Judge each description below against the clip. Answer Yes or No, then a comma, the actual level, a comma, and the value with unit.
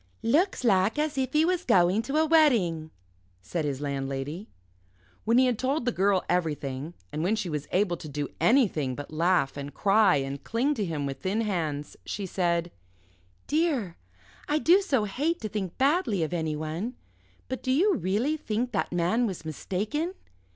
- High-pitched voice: Yes, high, 195 Hz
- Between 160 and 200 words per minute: Yes, average, 175 wpm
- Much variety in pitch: Yes, wide, 8.5 semitones